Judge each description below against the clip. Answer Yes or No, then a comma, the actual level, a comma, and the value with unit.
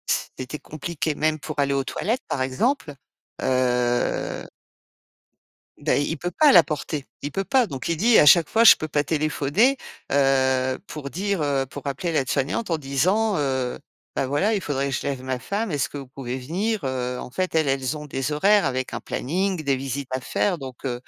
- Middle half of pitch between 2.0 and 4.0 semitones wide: No, average, 4.8 semitones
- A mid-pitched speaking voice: Yes, medium, 145 Hz